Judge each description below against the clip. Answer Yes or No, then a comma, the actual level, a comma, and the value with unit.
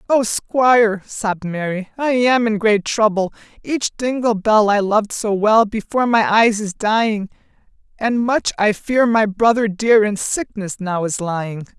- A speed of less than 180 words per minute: Yes, average, 170 wpm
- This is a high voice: Yes, high, 215 Hz